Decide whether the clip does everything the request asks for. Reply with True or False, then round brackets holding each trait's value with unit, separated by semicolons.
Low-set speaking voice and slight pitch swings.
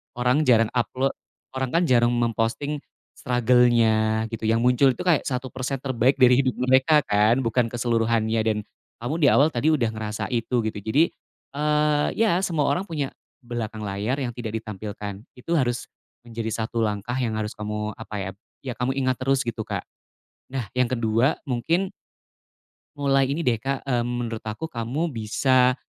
False (120 Hz; 3.2 semitones)